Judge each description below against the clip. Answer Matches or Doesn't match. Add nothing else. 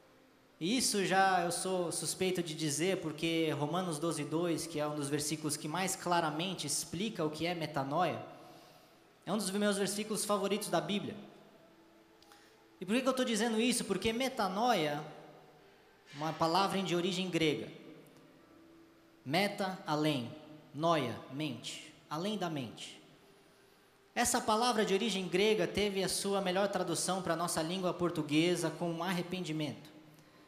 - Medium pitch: Matches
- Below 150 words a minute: Matches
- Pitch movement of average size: Matches